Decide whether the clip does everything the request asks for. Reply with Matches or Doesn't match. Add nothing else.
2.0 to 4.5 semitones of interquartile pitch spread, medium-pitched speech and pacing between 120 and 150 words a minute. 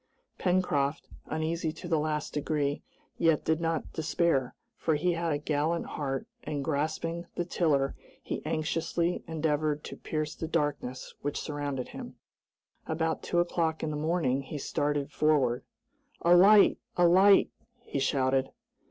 Matches